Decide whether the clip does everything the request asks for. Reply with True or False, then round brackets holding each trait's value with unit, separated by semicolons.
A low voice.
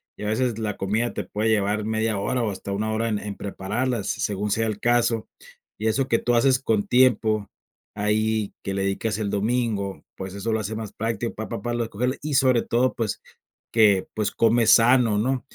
True (110 Hz)